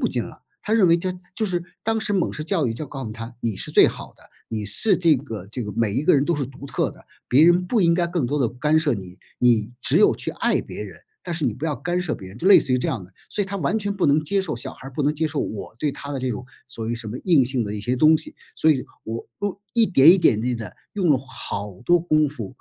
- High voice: No, medium, 145 Hz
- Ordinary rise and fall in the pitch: No, wide, 6.8 semitones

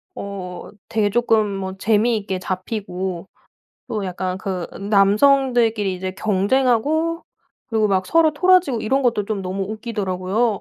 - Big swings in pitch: No, average, 4.0 semitones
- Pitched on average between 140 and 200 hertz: No, high, 210 Hz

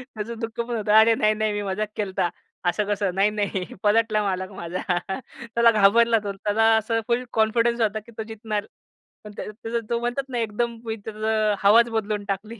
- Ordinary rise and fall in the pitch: No, narrow, 2.0 semitones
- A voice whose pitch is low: No, high, 215 Hz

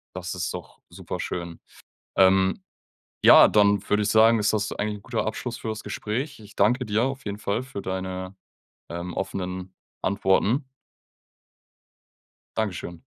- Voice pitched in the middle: No, low, 100 Hz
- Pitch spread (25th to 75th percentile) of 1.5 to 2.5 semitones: No, average, 2.9 semitones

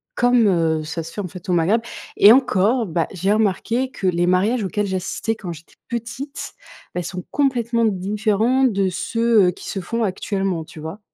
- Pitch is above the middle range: Yes, high, 200 Hz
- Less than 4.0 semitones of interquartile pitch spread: No, average, 4.4 semitones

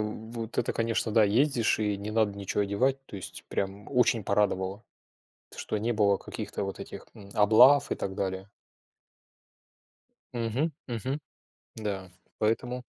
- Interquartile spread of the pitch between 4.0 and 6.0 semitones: No, average, 2.9 semitones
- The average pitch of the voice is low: Yes, low, 110 Hz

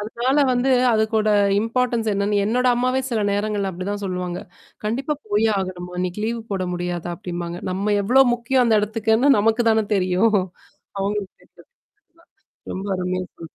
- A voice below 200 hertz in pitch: No, high, 210 Hz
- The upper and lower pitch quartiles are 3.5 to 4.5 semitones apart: Yes, average, 3.9 semitones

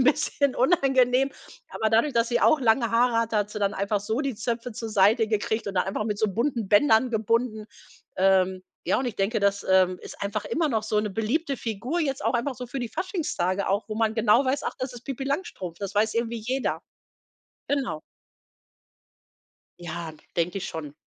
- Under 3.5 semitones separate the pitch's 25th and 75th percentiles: No, average, 4.1 semitones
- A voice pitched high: Yes, high, 225 Hz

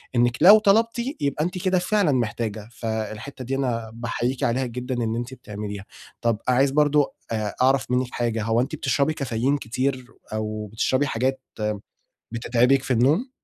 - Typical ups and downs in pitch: Yes, average, 3.4 semitones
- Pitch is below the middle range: Yes, low, 125 Hz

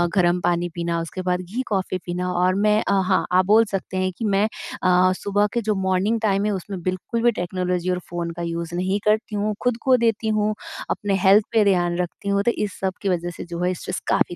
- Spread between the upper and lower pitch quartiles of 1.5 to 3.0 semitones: Yes, average, 2.7 semitones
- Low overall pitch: No, medium, 185 Hz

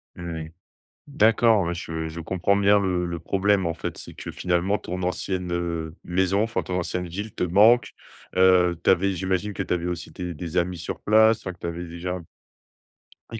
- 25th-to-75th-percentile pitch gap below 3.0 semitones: Yes, narrow, 2.4 semitones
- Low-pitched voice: Yes, very low, 90 Hz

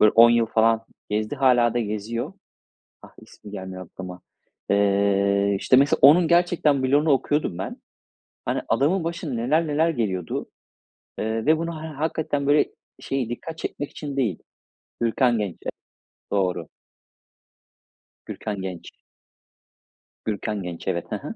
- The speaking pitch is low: Yes, low, 115 Hz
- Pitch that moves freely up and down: Yes, wide, 6.4 semitones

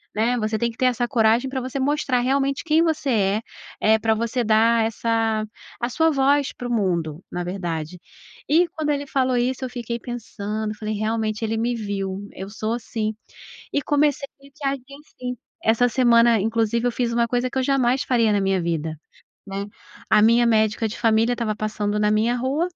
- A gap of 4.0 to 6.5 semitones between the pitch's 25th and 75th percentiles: No, average, 3.0 semitones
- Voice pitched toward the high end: Yes, high, 230 Hz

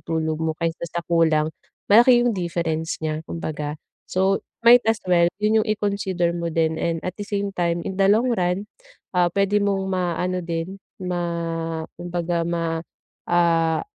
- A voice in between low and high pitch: Yes, medium, 175 Hz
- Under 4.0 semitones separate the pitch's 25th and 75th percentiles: Yes, average, 2.9 semitones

